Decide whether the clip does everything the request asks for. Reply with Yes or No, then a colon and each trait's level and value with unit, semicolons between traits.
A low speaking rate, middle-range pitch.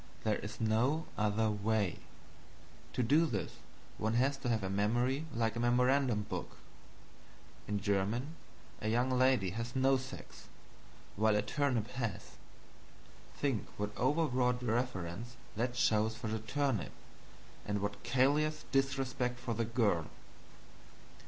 No: slow, 130 wpm; low, 120 Hz